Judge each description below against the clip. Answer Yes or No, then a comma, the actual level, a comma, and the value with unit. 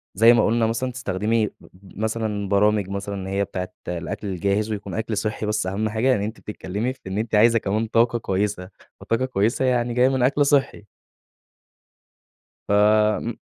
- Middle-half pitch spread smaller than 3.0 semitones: Yes, narrow, 2.6 semitones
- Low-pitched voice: Yes, low, 105 Hz